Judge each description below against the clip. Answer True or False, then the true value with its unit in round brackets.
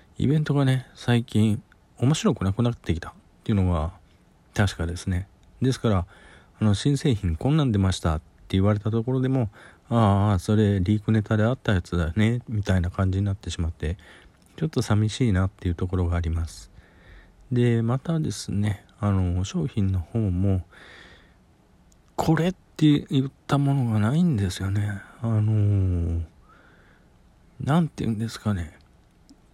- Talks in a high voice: False (105 Hz)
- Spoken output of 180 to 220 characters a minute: False (305 characters per minute)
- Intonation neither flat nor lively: True (4.9 semitones)